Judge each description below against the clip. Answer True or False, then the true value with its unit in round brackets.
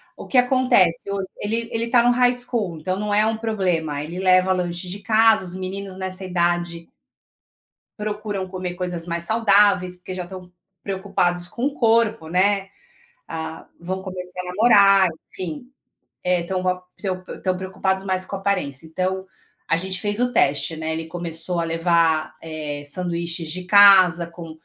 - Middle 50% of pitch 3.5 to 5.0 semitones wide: False (2.8 semitones)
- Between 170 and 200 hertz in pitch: True (185 Hz)